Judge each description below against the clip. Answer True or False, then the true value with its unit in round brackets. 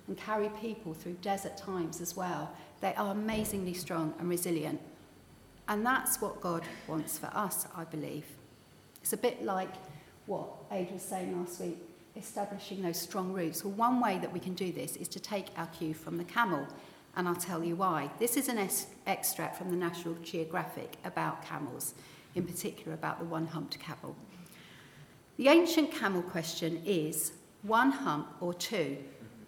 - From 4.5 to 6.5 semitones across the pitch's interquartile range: False (3.4 semitones)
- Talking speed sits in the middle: True (175 wpm)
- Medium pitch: True (180 Hz)